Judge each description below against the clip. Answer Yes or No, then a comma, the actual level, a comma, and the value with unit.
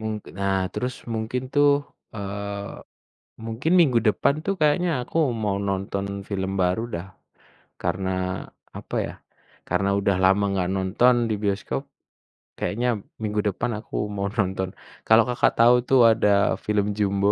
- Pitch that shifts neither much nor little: Yes, average, 3.3 semitones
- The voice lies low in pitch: Yes, low, 105 Hz